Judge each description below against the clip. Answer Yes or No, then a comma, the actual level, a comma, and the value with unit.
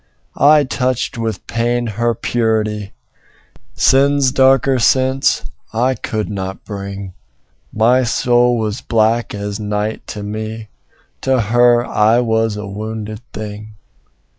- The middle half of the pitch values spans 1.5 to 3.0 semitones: Yes, narrow, 2.5 semitones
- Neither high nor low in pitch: No, low, 110 Hz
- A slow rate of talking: Yes, slow, 115 wpm